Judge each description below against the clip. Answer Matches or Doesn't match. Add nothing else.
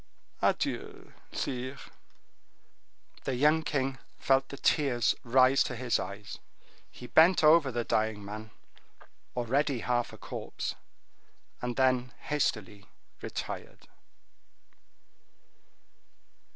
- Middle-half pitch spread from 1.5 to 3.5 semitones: Matches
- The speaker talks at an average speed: Doesn't match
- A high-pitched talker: Doesn't match